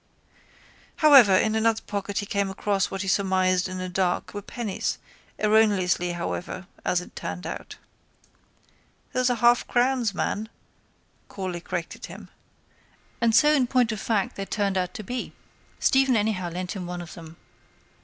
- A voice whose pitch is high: Yes, high, 200 Hz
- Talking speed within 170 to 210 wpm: No, average, 155 wpm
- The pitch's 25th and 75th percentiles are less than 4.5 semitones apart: Yes, average, 3.6 semitones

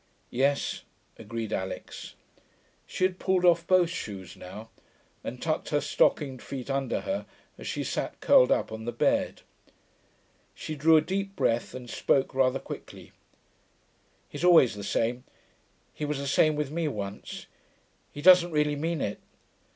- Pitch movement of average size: No, wide, 6.0 semitones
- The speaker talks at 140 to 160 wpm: Yes, average, 150 wpm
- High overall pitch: No, medium, 140 Hz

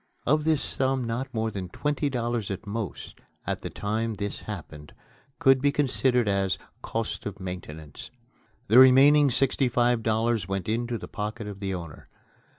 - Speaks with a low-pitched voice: Yes, low, 115 Hz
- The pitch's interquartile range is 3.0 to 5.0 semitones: Yes, average, 4.7 semitones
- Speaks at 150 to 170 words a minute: Yes, average, 160 wpm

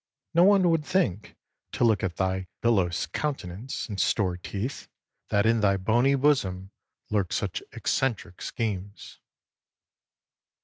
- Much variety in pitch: Yes, wide, 6.1 semitones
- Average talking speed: No, slow, 125 wpm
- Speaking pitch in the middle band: No, low, 105 Hz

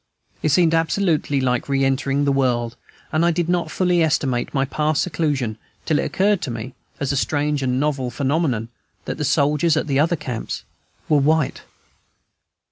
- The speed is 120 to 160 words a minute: No, average, 175 wpm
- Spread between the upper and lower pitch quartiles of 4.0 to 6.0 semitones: No, average, 3.3 semitones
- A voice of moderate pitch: Yes, medium, 145 Hz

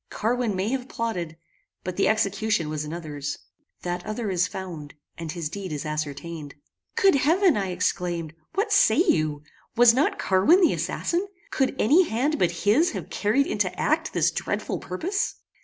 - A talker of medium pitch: No, high, 200 Hz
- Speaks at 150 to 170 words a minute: Yes, average, 160 wpm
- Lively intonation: Yes, wide, 8.0 semitones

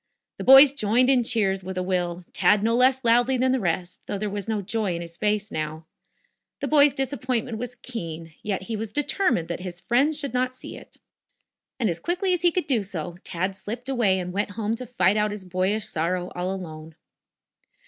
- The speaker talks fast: Yes, fast, 210 wpm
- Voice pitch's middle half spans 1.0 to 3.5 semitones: No, wide, 5.5 semitones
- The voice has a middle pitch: No, high, 210 Hz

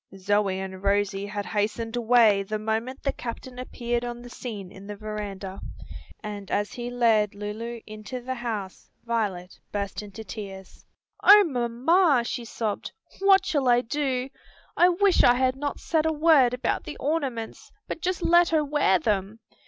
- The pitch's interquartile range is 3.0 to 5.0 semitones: Yes, average, 4.1 semitones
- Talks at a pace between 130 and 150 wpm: No, average, 165 wpm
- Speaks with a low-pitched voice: No, high, 235 Hz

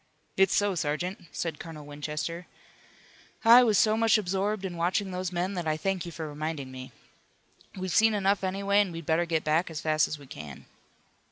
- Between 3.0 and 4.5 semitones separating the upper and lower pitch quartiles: Yes, average, 4.0 semitones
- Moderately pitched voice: Yes, medium, 175 Hz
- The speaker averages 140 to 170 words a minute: No, average, 190 wpm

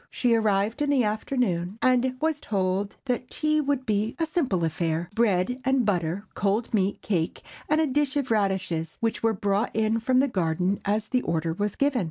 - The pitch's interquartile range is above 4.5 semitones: Yes, average, 5.1 semitones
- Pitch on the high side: Yes, high, 220 Hz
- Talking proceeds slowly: No, average, 185 wpm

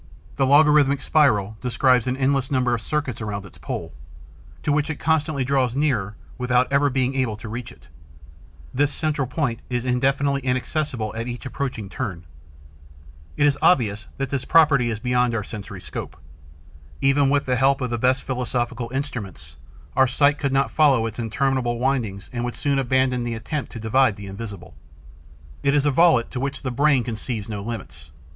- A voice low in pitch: Yes, low, 125 Hz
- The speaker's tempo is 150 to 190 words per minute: Yes, average, 180 wpm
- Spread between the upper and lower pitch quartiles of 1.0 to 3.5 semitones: Yes, average, 3.2 semitones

